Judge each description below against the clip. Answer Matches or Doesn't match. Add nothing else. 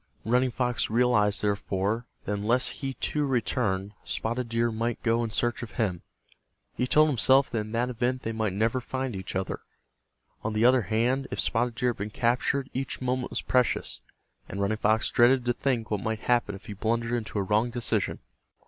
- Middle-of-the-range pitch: Doesn't match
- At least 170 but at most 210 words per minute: Matches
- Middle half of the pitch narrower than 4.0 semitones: Matches